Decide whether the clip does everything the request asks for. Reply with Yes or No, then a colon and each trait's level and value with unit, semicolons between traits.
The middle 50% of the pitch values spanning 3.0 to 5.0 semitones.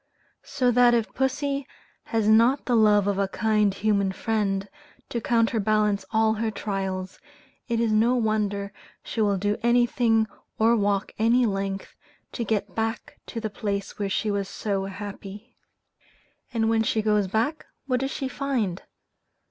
No: narrow, 2.6 semitones